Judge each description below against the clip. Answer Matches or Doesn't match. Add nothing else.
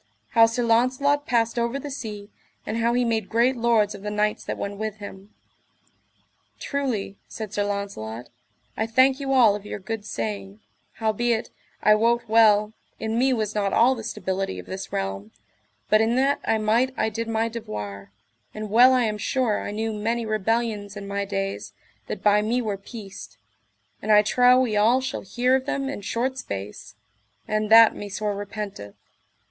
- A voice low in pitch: Doesn't match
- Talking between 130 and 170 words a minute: Doesn't match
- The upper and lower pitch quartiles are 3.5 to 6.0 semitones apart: Doesn't match